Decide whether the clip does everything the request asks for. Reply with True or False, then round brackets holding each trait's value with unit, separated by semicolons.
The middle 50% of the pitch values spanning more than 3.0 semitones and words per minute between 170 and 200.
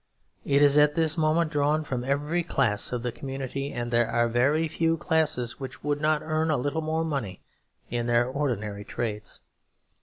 True (4.4 semitones; 180 wpm)